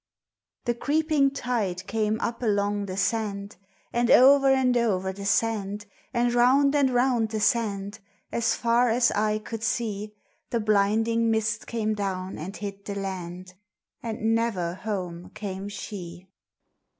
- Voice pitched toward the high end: Yes, high, 215 Hz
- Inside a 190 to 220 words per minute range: No, average, 140 wpm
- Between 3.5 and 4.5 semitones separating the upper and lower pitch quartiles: No, average, 3.1 semitones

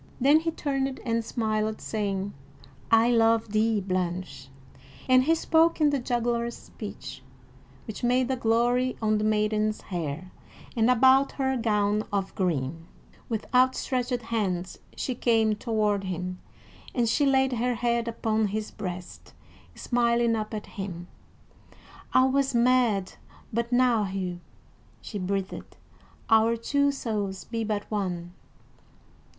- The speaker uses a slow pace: Yes, slow, 130 wpm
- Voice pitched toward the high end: Yes, high, 225 Hz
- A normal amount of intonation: Yes, average, 3.5 semitones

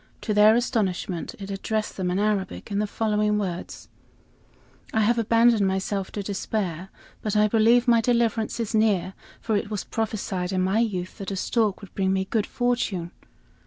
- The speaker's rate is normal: Yes, average, 175 wpm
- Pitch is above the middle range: Yes, high, 210 Hz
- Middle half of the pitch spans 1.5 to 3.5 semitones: Yes, average, 2.7 semitones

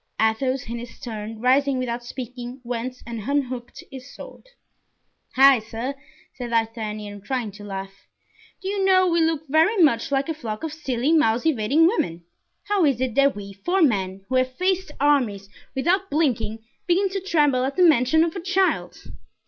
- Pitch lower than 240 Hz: No, very high, 260 Hz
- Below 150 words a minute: No, average, 175 wpm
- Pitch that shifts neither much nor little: No, wide, 6.0 semitones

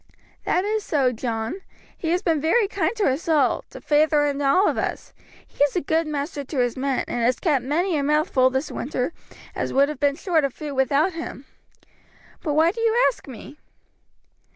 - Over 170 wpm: Yes, fast, 205 wpm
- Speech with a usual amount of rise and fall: Yes, average, 3.7 semitones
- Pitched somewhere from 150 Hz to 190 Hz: No, very high, 295 Hz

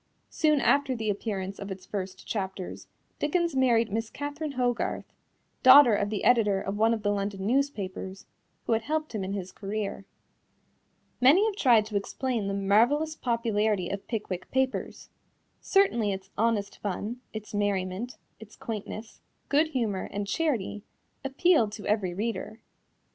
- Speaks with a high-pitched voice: Yes, high, 220 Hz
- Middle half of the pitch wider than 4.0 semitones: Yes, average, 4.6 semitones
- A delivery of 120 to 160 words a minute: Yes, average, 150 wpm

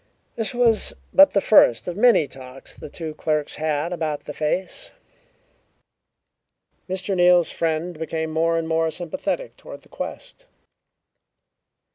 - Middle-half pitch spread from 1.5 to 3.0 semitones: No, average, 4.0 semitones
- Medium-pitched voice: Yes, medium, 165 Hz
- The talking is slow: Yes, slow, 130 wpm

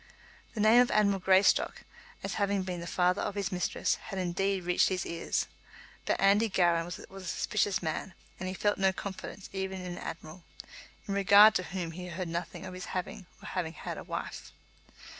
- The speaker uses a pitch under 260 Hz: Yes, medium, 185 Hz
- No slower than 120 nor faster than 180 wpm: No, average, 190 wpm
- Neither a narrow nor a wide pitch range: No, narrow, 2.0 semitones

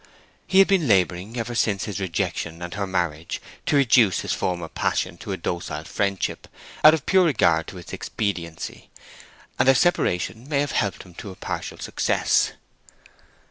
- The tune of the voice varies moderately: No, wide, 7.0 semitones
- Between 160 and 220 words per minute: Yes, average, 170 wpm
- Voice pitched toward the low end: Yes, low, 100 Hz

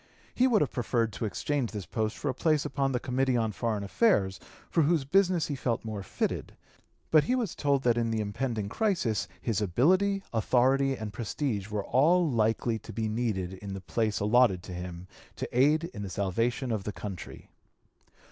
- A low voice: Yes, low, 120 Hz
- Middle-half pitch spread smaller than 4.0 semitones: No, average, 5.2 semitones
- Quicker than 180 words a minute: Yes, average, 190 wpm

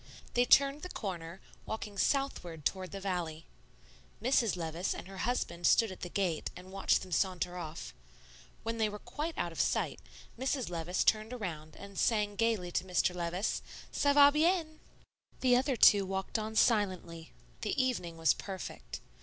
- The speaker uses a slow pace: No, average, 165 wpm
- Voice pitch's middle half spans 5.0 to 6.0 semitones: Yes, average, 5.3 semitones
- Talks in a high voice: Yes, high, 195 Hz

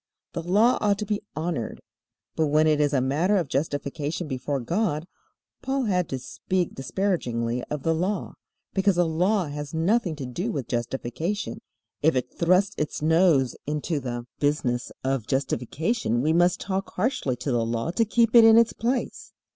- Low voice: No, medium, 160 Hz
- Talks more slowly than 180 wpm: Yes, average, 170 wpm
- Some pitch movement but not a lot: No, wide, 6.2 semitones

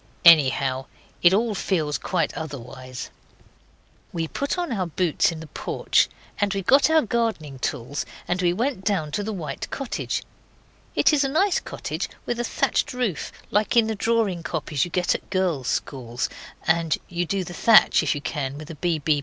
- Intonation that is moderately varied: No, wide, 6.5 semitones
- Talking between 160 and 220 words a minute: Yes, average, 180 wpm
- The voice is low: No, medium, 175 Hz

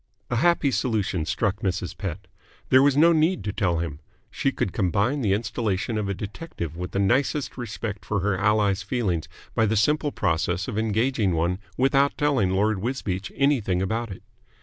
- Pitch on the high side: No, low, 105 Hz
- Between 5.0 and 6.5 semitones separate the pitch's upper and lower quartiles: Yes, wide, 5.4 semitones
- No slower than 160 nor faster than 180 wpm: Yes, average, 175 wpm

